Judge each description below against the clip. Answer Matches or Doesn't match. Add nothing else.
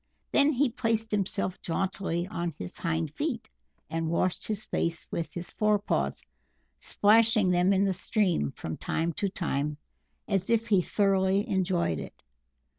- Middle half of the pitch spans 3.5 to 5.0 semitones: Matches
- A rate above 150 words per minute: Doesn't match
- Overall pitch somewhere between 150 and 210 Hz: Matches